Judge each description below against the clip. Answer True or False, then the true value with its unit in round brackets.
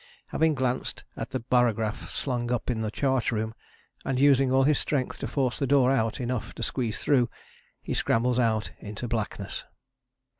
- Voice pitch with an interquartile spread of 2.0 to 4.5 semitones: True (2.8 semitones)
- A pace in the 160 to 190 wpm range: True (175 wpm)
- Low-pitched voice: True (125 Hz)